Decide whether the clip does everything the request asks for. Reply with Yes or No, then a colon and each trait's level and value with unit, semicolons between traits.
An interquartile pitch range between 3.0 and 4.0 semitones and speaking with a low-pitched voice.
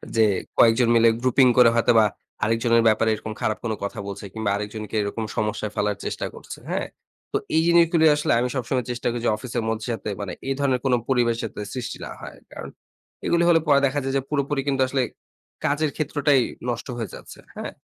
Yes: average, 3.7 semitones; low, 120 Hz